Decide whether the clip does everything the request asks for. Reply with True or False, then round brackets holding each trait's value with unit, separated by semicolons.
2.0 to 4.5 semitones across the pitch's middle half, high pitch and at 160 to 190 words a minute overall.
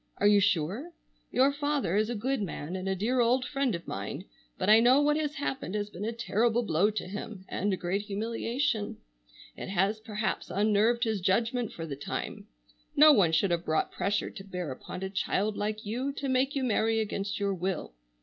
False (4.2 semitones; 210 Hz; 205 wpm)